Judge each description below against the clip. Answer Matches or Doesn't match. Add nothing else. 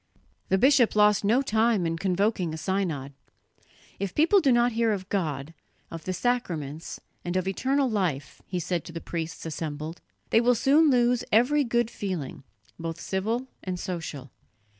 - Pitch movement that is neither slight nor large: Doesn't match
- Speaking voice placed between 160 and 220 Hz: Matches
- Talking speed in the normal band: Matches